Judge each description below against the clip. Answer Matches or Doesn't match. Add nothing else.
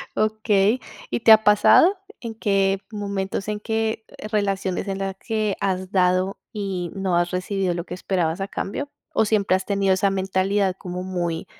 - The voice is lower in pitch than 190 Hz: Doesn't match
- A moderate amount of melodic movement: Doesn't match